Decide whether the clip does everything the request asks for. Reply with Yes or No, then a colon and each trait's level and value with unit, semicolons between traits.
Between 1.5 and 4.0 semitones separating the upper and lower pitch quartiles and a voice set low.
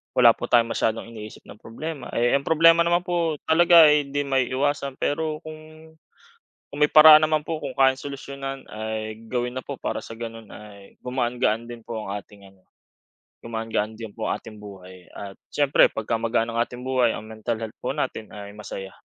No: average, 4.7 semitones; low, 120 Hz